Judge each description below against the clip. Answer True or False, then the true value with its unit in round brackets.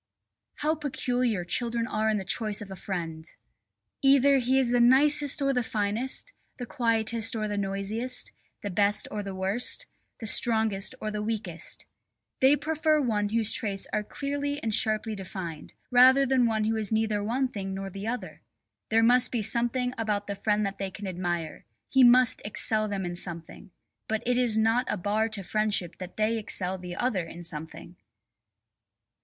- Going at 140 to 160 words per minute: False (175 wpm)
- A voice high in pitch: True (220 Hz)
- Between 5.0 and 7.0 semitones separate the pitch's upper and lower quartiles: False (3.8 semitones)